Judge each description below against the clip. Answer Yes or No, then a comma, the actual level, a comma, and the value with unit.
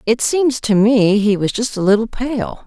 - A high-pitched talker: Yes, high, 220 Hz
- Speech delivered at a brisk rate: Yes, fast, 225 wpm